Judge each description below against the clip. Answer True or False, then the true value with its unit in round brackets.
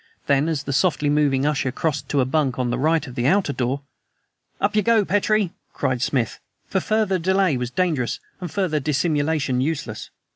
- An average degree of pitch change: False (5.7 semitones)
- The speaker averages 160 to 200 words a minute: True (185 wpm)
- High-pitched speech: False (150 Hz)